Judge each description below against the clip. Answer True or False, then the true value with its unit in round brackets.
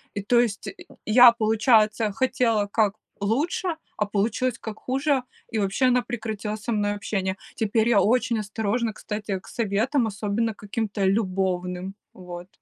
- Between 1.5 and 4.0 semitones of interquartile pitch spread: True (2.7 semitones)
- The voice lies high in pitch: True (215 Hz)